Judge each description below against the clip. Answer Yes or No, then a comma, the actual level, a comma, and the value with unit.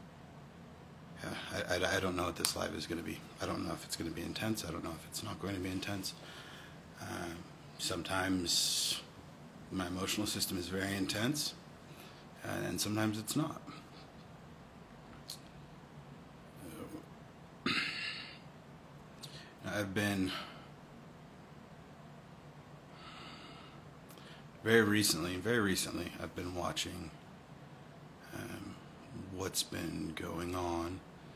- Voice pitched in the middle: No, very low, 95 Hz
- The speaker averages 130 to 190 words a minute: No, slow, 110 wpm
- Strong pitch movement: No, average, 3.0 semitones